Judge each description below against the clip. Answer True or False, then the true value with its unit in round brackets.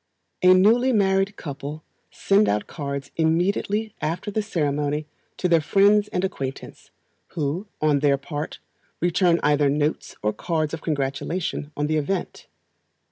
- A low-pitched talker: False (160 Hz)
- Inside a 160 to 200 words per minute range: False (135 wpm)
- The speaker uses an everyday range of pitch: True (4.7 semitones)